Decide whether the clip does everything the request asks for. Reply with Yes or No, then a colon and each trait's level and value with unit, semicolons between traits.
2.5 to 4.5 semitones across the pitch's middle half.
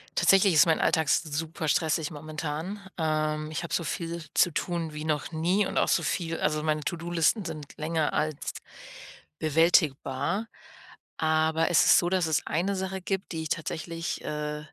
No: narrow, 2.0 semitones